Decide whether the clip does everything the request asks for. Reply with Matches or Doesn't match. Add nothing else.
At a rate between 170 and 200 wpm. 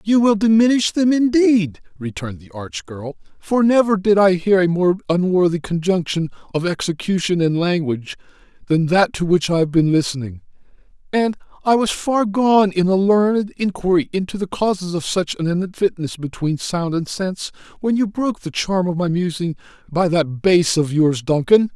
Matches